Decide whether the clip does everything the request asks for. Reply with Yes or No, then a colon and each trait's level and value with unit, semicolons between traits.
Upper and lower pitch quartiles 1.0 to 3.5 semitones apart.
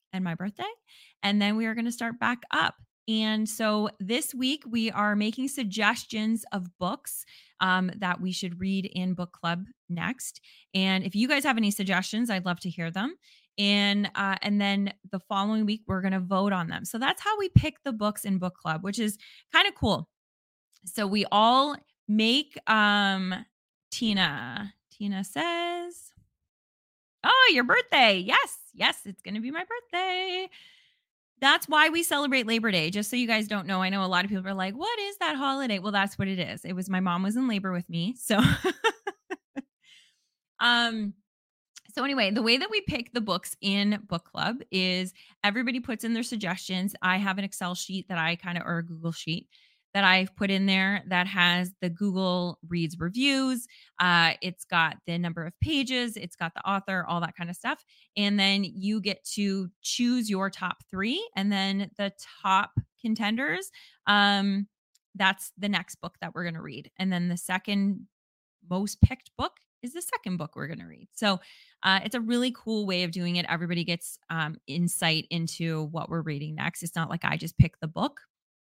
No: average, 4.5 semitones